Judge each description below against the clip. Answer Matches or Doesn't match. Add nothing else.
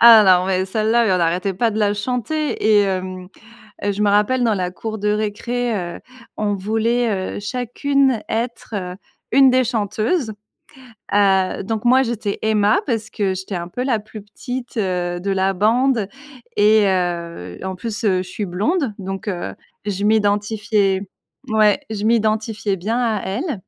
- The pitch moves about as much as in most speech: Matches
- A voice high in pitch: Matches